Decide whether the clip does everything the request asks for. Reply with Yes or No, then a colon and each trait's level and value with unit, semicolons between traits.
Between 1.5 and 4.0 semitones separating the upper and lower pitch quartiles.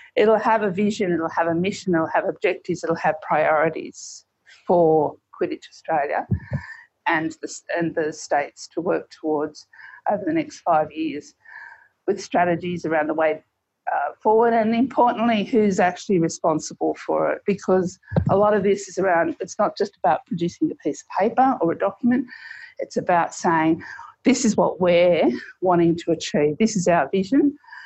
No: average, 5.2 semitones